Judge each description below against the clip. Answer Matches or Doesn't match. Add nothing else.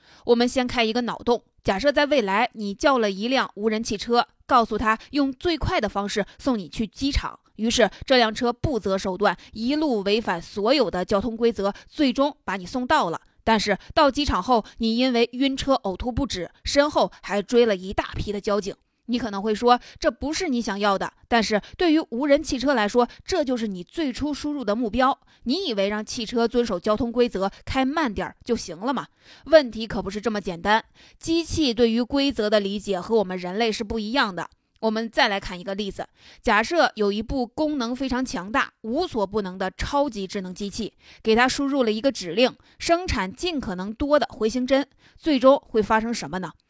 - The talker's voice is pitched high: Matches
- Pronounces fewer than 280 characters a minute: Doesn't match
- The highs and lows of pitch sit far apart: Doesn't match